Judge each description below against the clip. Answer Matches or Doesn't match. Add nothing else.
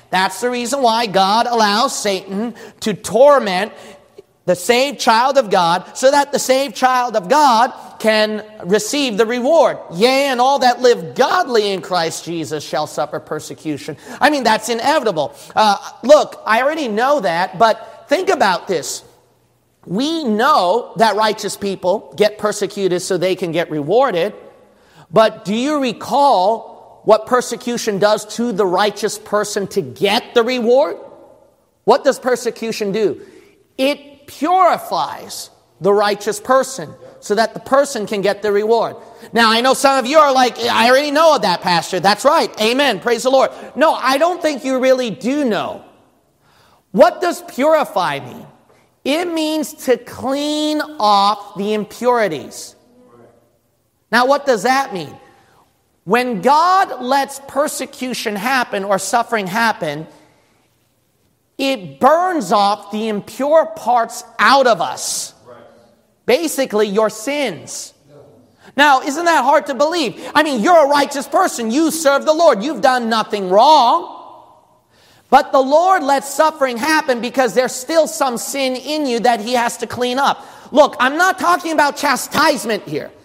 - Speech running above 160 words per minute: Doesn't match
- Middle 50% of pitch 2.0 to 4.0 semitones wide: Doesn't match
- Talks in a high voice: Matches